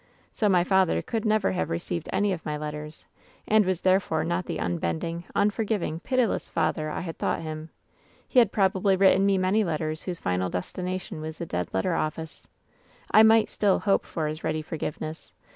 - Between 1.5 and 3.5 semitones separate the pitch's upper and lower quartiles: No, average, 4.2 semitones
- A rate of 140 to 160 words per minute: No, average, 190 wpm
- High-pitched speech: No, medium, 175 Hz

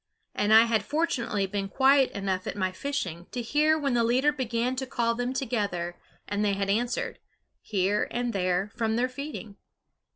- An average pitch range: Yes, average, 4.6 semitones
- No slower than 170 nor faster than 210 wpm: Yes, average, 175 wpm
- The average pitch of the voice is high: Yes, high, 230 Hz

